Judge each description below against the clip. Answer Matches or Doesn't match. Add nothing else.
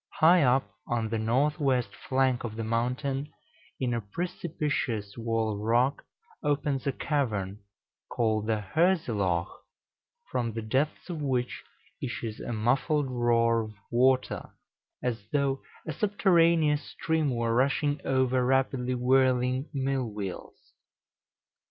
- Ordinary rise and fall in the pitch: Matches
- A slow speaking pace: Matches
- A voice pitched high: Doesn't match